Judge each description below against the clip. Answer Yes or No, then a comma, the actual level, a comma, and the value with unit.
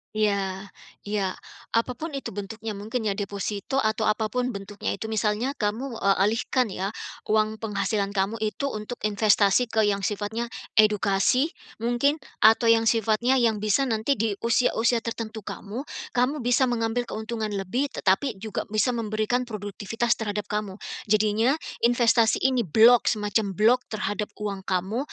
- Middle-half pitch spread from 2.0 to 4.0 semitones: Yes, narrow, 2.5 semitones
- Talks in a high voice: Yes, high, 220 Hz